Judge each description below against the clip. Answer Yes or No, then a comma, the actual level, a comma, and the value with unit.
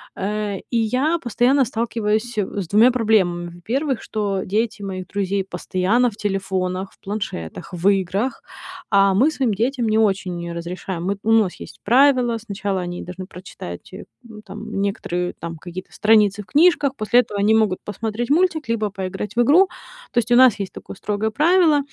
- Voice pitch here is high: Yes, high, 210 Hz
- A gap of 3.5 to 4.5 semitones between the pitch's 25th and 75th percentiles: Yes, average, 4.0 semitones